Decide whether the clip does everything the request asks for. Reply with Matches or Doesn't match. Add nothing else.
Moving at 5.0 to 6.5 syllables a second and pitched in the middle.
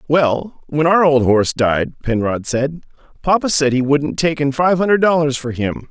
Doesn't match